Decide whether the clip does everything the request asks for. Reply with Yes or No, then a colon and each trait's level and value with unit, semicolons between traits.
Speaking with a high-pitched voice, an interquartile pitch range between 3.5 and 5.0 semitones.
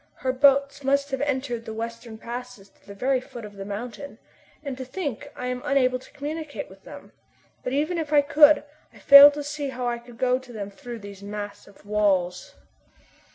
Yes: very high, 255 Hz; average, 4.2 semitones